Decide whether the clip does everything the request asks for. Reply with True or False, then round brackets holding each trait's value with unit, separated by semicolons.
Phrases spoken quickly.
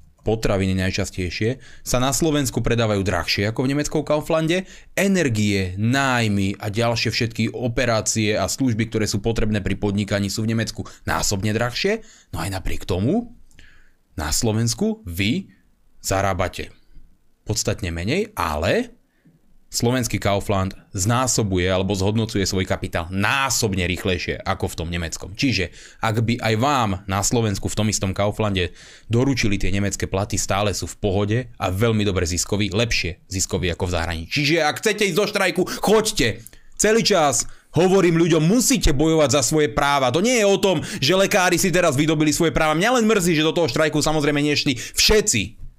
False (155 wpm)